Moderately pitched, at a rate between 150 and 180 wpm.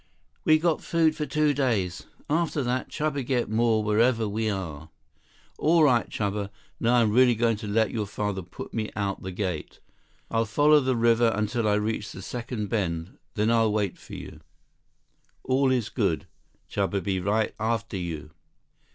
No: low, 110 Hz; average, 170 wpm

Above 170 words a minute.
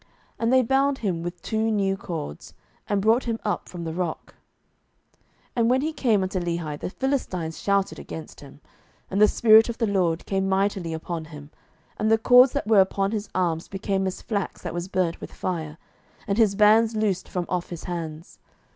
Yes: average, 195 wpm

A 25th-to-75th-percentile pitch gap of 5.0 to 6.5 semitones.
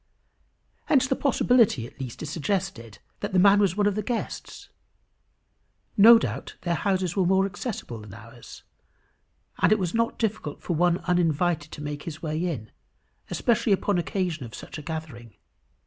Yes: wide, 5.4 semitones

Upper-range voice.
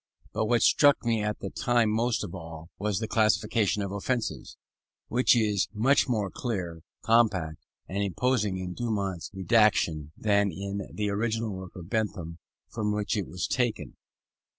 No: low, 105 Hz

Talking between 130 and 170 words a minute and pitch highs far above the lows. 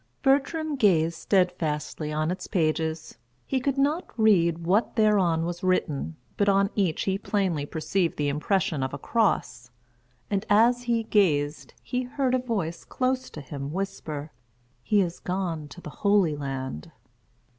Yes: average, 150 wpm; wide, 5.7 semitones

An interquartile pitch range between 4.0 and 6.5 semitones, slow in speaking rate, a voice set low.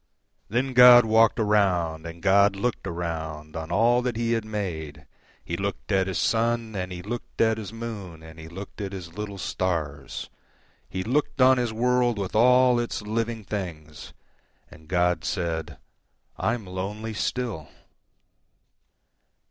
Yes: average, 5.2 semitones; slow, 125 wpm; low, 100 Hz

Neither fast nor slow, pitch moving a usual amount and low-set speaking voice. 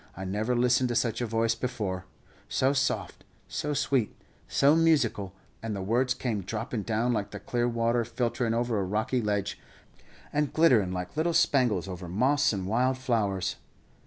Yes: average, 165 wpm; average, 3.7 semitones; low, 115 Hz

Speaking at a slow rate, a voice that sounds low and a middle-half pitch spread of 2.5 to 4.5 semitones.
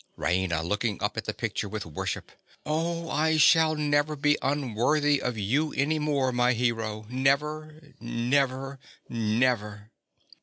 No: slow, 130 wpm; low, 130 Hz; average, 5.0 semitones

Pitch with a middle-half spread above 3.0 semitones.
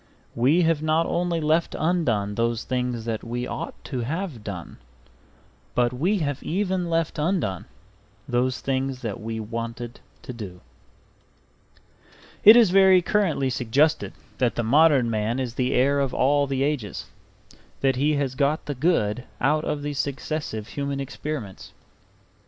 Yes: average, 4.8 semitones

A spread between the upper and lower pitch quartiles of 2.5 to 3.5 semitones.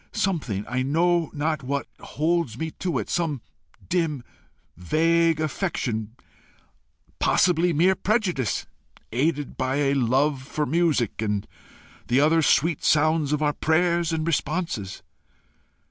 No: average, 4.1 semitones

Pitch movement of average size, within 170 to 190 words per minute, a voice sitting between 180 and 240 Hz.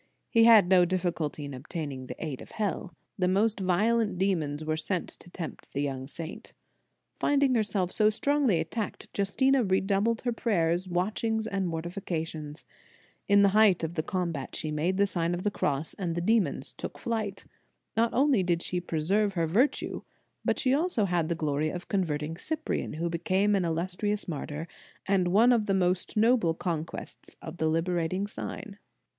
Yes: average, 4.4 semitones; average, 175 wpm; medium, 185 Hz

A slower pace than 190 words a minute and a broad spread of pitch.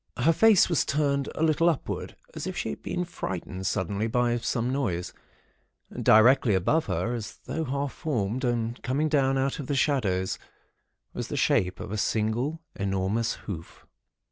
Yes: average, 165 wpm; wide, 5.7 semitones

